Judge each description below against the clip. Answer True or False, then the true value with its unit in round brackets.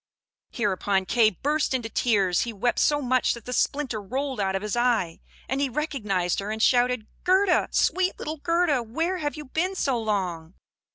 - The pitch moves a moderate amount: False (6.1 semitones)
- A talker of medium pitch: False (245 Hz)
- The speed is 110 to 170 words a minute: False (180 wpm)